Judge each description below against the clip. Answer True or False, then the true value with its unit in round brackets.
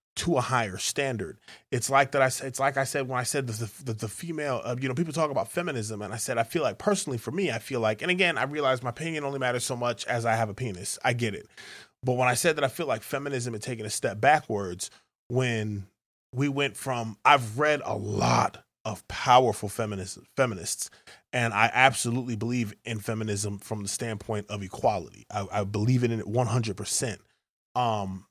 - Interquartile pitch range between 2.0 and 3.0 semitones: False (3.6 semitones)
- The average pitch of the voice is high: False (120 Hz)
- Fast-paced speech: True (215 wpm)